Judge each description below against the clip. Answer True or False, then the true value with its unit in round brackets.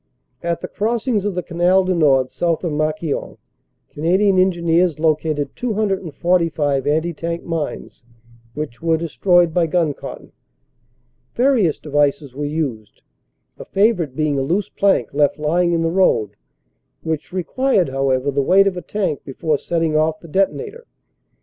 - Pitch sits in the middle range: True (165 Hz)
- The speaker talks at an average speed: True (145 wpm)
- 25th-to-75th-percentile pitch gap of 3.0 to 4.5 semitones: True (3.7 semitones)